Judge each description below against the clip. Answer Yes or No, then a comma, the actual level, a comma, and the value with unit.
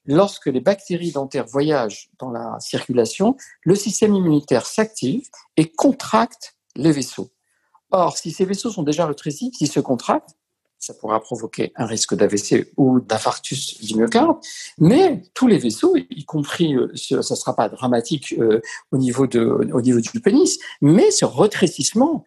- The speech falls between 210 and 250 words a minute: No, average, 155 wpm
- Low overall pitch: No, medium, 150 Hz